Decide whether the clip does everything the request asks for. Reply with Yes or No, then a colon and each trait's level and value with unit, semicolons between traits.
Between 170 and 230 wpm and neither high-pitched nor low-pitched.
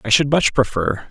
No: fast, 215 wpm; low, 120 Hz